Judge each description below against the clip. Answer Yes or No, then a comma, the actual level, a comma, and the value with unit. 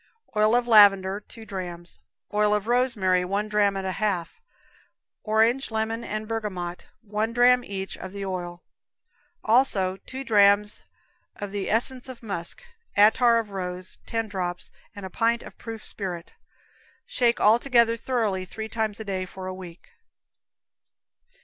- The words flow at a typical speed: Yes, average, 150 wpm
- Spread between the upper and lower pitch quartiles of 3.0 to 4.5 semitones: Yes, average, 3.3 semitones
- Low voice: No, high, 210 Hz